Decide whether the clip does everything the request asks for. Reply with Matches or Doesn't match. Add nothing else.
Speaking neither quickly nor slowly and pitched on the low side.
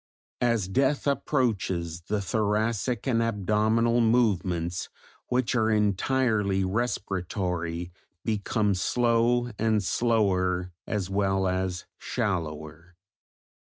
Doesn't match